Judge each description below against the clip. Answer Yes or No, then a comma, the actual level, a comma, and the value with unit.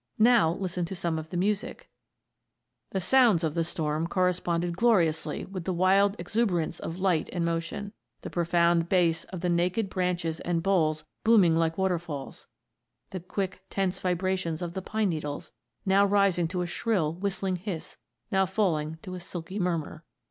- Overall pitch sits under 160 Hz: No, medium, 180 Hz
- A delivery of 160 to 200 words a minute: Yes, average, 165 wpm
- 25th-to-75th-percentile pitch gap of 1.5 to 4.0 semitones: Yes, narrow, 2.5 semitones